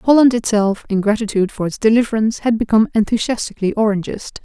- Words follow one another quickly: No, average, 150 wpm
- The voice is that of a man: No, female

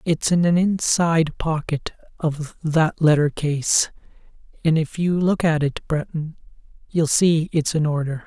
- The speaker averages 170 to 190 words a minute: No, average, 150 wpm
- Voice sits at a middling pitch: Yes, medium, 160 Hz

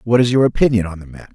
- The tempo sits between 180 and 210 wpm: No, fast, 310 wpm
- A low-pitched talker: Yes, low, 110 Hz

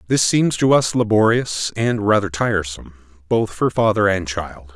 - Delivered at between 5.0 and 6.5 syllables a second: No, 4.7 syllables/s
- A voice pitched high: No, low, 105 Hz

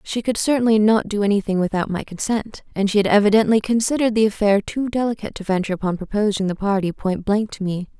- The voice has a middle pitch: No, high, 210 Hz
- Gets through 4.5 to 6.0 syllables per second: No, 6.5 syllables/s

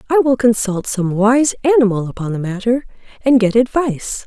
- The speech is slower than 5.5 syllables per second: Yes, 5.3 syllables/s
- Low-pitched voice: No, high, 230 Hz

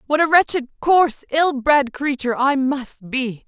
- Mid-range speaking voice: No, very high, 275 Hz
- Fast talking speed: No, average, 175 wpm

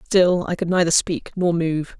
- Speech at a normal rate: No, fast, 210 wpm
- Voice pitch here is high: No, medium, 175 Hz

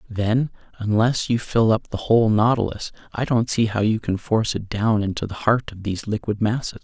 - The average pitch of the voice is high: No, low, 110 Hz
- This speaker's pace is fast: Yes, fast, 210 wpm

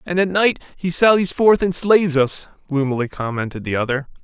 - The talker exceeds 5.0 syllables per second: Yes, 5.3 syllables/s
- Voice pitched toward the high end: No, medium, 160 Hz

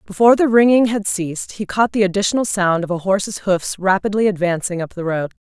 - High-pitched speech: Yes, high, 195 Hz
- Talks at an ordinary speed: No, fast, 210 wpm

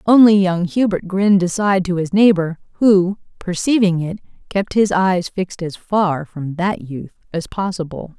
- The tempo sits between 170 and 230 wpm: No, average, 160 wpm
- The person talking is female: Yes, female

